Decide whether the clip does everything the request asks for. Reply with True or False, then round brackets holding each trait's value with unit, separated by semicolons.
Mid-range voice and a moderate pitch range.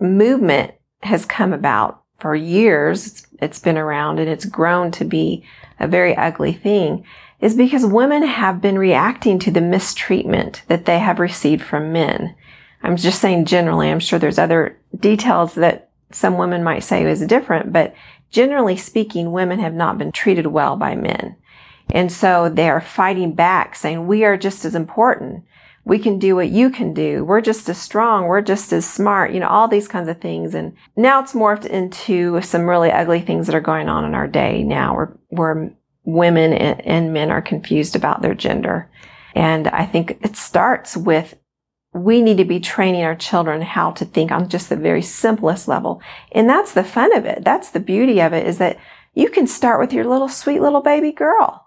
True (180 Hz; 4.1 semitones)